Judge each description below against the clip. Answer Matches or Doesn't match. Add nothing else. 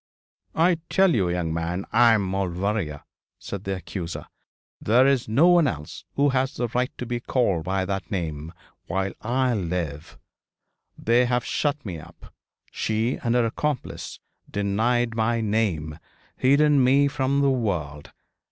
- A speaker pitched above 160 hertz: Doesn't match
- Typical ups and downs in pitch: Doesn't match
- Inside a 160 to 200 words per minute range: Doesn't match